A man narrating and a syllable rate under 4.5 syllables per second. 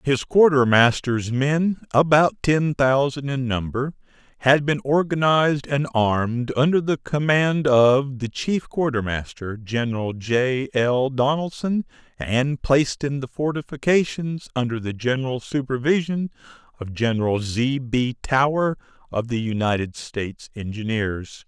Yes: male; 4.2 syllables/s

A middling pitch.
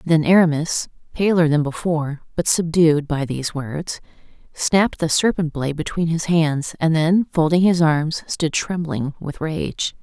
Yes: medium, 160 Hz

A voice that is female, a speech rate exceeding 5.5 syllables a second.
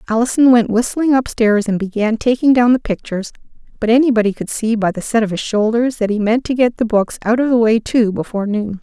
Yes: female; 5.9 syllables/s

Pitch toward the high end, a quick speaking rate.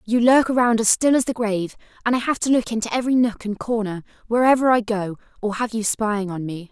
Yes: high, 225 Hz; fast, 240 wpm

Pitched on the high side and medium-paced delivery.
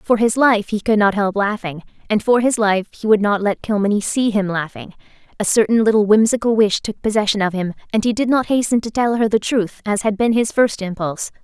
No: high, 215 Hz; fast, 235 wpm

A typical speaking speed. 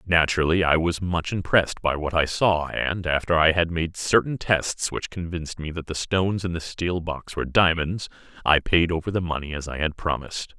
No: fast, 210 wpm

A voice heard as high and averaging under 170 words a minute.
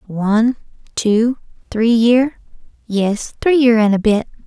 Yes: high, 225 Hz; slow, 135 wpm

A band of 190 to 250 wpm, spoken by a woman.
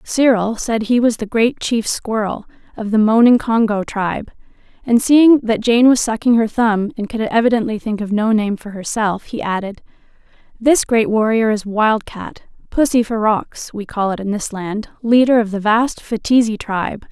No: average, 180 wpm; female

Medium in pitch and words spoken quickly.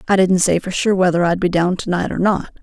Yes: medium, 180 Hz; fast, 275 wpm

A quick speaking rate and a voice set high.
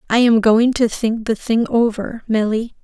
No: average, 190 wpm; high, 225 Hz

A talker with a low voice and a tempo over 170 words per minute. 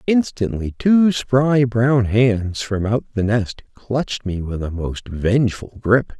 No: low, 115 Hz; average, 155 wpm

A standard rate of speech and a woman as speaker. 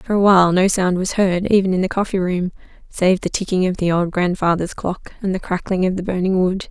No: fast, 240 wpm; female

